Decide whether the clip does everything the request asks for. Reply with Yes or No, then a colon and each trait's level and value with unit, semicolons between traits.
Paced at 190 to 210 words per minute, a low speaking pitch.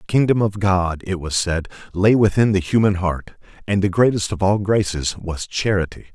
Yes: average, 195 wpm; very low, 95 Hz